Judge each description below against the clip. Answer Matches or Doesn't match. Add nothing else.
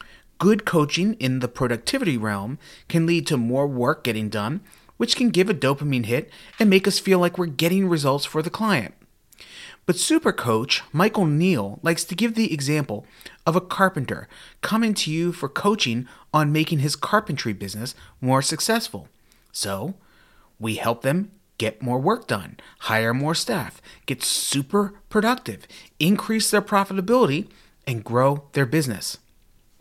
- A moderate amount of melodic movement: Doesn't match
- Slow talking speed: Doesn't match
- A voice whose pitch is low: Doesn't match